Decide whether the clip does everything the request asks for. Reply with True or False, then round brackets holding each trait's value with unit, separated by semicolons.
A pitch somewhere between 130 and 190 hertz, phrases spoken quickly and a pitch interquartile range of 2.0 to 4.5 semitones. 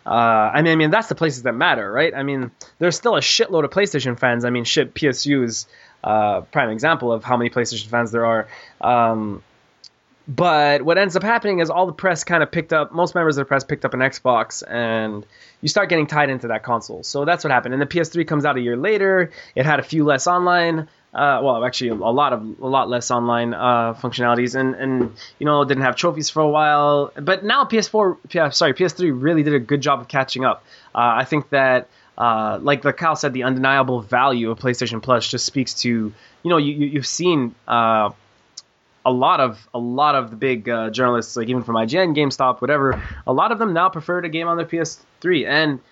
False (135 Hz; 225 wpm; 4.9 semitones)